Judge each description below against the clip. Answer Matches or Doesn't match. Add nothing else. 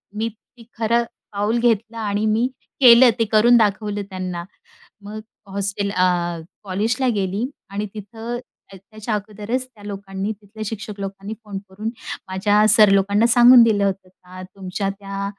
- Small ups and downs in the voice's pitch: Matches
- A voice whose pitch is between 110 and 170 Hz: Doesn't match